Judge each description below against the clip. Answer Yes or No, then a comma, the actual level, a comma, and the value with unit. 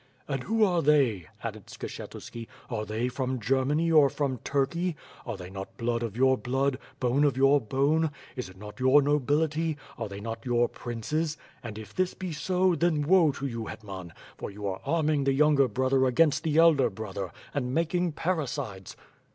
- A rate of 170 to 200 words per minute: Yes, average, 185 wpm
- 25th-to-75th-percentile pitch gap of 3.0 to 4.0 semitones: No, average, 4.9 semitones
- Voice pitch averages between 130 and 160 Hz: Yes, low, 135 Hz